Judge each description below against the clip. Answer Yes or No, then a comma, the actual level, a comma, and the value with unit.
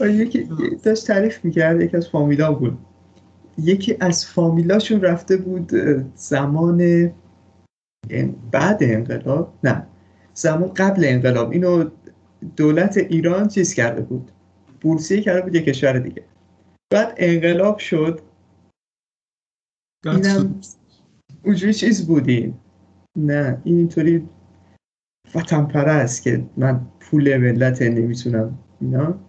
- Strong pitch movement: Yes, wide, 6.4 semitones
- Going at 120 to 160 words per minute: No, slow, 105 wpm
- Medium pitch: Yes, medium, 160 Hz